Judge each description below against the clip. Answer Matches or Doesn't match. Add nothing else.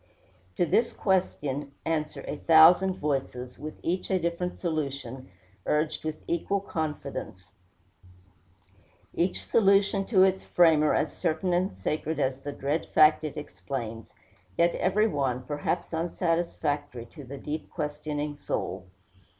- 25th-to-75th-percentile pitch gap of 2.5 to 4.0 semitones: Matches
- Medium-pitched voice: Matches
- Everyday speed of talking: Doesn't match